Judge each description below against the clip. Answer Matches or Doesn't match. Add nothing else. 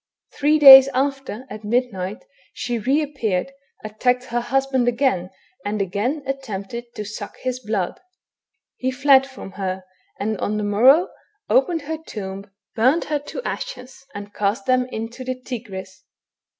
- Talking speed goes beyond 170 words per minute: Doesn't match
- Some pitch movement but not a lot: Matches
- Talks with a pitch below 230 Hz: Doesn't match